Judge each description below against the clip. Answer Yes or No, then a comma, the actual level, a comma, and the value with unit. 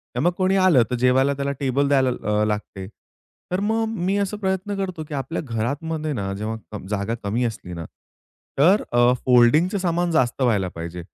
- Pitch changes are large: Yes, wide, 8.0 semitones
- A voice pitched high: No, low, 135 Hz